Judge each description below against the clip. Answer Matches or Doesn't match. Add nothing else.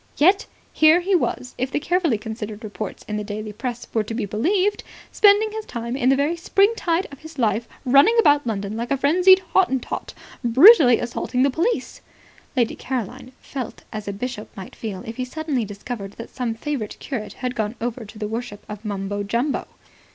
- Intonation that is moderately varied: Doesn't match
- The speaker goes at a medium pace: Matches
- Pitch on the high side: Matches